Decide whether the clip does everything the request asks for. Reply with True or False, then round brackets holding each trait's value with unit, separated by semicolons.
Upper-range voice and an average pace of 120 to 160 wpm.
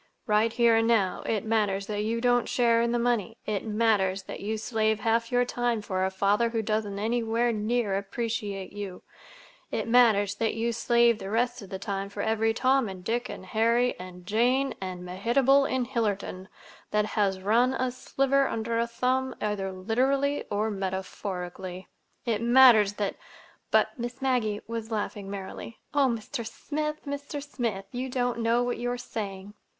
False (225 Hz; 175 wpm)